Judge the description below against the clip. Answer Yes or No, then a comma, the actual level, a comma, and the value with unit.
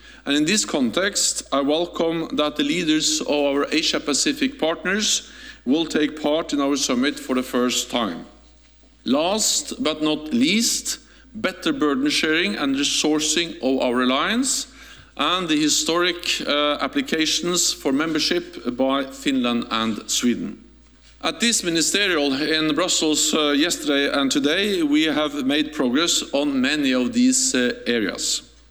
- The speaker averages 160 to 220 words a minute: No, average, 140 wpm